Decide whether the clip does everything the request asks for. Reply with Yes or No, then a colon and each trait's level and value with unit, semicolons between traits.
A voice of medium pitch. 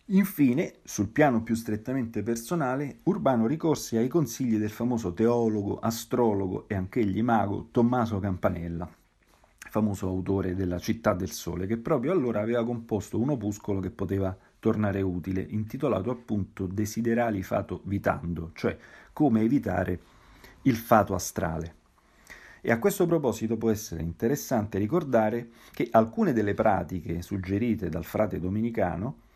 No: low, 110 Hz